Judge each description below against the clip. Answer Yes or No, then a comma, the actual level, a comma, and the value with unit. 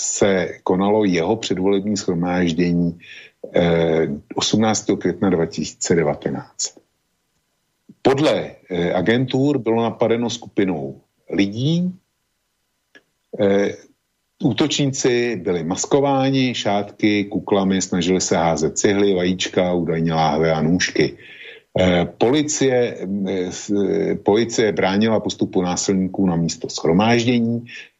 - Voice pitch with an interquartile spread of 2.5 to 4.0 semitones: No, average, 4.6 semitones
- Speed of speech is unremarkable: No, slow, 75 wpm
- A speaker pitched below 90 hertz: No, low, 100 Hz